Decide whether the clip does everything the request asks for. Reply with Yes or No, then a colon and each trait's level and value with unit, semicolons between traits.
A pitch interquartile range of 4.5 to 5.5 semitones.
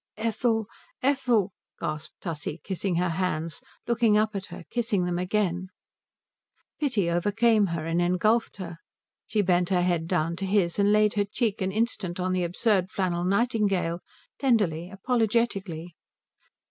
No: average, 3.7 semitones